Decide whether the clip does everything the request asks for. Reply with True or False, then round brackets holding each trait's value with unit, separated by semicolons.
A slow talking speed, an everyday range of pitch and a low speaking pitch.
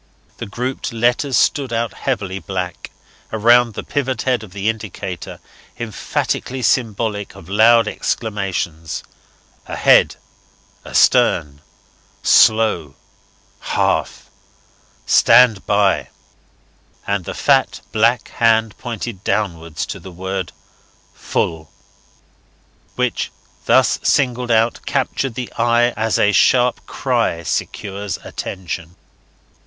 True (100 wpm; 3.8 semitones; 110 Hz)